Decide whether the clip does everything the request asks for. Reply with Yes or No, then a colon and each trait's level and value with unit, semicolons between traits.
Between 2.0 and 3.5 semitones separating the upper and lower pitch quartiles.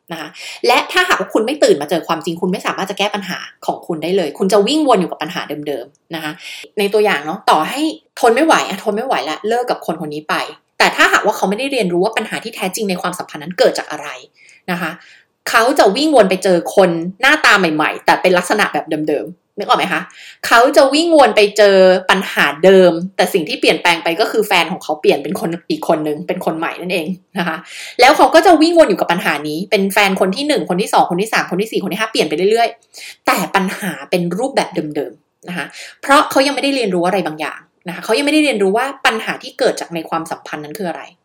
No: wide, 5.5 semitones